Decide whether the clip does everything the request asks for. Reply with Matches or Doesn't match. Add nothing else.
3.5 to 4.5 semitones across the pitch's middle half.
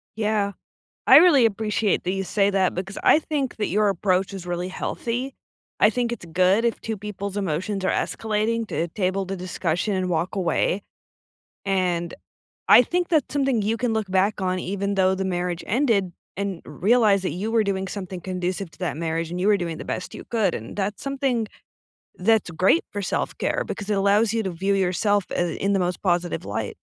Doesn't match